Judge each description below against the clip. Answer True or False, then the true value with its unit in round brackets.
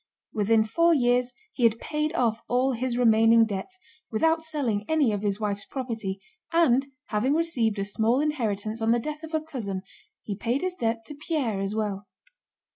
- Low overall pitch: False (235 Hz)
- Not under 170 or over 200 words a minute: True (180 wpm)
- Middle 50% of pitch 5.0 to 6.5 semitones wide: True (5.5 semitones)